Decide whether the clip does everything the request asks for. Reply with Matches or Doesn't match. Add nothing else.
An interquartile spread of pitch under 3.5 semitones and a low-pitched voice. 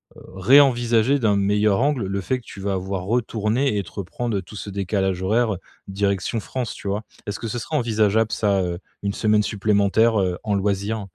Matches